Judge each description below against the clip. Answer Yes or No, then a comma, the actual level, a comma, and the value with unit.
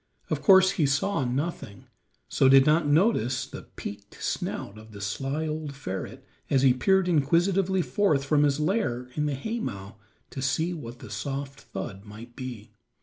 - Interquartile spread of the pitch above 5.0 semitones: Yes, wide, 5.5 semitones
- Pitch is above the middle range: No, medium, 140 Hz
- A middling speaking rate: Yes, average, 165 wpm